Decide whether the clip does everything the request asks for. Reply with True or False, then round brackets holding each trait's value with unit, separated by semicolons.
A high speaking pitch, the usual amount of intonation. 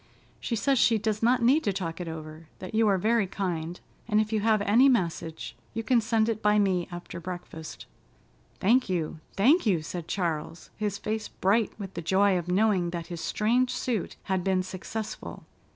True (200 Hz; 4.0 semitones)